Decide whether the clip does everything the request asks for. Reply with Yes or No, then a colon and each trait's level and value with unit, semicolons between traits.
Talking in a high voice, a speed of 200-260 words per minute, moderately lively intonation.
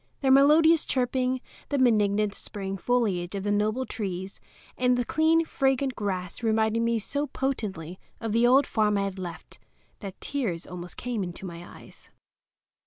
No: high, 220 Hz; average, 160 wpm; average, 5.0 semitones